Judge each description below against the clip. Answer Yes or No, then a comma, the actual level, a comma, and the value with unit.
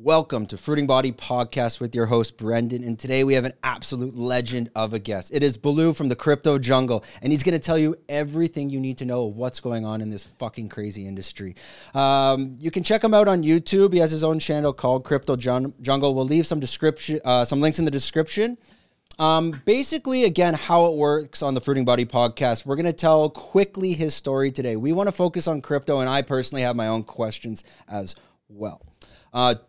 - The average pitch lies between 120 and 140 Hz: Yes, low, 135 Hz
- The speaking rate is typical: No, fast, 215 wpm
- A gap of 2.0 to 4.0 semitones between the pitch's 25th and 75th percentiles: No, average, 4.6 semitones